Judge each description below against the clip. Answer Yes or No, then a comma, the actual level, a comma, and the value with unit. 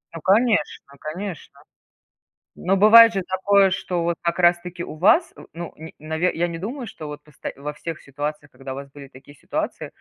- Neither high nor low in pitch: Yes, medium, 170 Hz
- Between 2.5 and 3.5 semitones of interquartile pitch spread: No, average, 4.6 semitones